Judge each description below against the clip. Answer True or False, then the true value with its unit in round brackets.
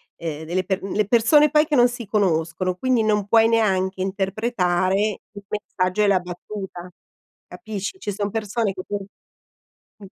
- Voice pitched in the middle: False (200 Hz)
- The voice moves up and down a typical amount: True (3.1 semitones)